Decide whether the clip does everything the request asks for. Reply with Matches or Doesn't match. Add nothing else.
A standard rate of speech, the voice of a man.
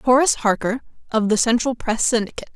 Doesn't match